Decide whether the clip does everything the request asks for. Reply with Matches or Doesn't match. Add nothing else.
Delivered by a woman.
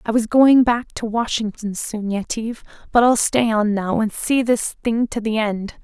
Matches